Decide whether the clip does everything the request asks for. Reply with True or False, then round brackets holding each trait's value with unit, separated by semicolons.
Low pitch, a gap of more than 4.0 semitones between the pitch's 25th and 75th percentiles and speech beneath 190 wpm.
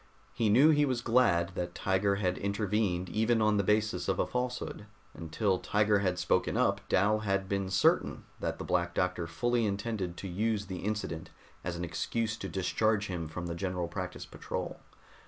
False (100 Hz; 3.1 semitones; 180 wpm)